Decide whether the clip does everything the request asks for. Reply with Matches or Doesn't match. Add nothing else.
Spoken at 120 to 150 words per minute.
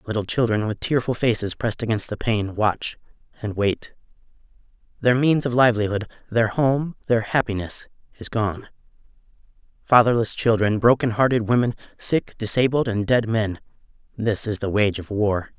Matches